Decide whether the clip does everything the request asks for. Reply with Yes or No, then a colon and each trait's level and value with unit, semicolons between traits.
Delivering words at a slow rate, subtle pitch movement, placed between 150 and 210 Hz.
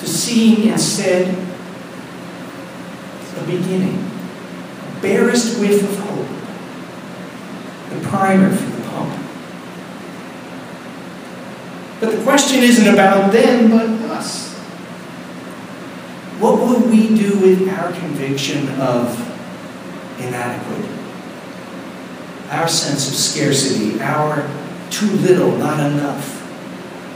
No: slow, 90 wpm; average, 5.2 semitones; high, 190 Hz